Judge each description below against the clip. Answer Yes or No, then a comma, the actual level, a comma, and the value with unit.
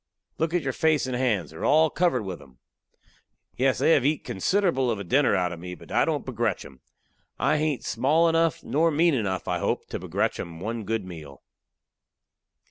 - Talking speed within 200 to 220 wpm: Yes, fast, 205 wpm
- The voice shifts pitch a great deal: Yes, wide, 9.0 semitones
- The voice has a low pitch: Yes, low, 130 Hz